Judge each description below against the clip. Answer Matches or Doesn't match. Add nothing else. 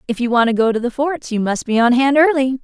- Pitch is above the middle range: Matches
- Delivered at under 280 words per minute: Doesn't match